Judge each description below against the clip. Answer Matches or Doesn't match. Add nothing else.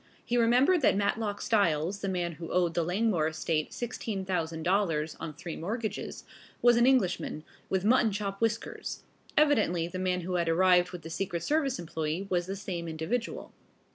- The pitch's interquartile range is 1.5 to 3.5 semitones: Doesn't match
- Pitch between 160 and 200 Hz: Matches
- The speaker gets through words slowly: Doesn't match